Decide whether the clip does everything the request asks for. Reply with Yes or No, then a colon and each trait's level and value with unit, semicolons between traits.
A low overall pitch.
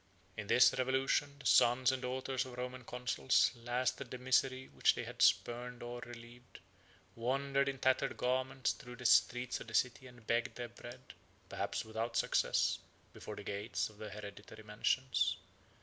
Yes: low, 125 Hz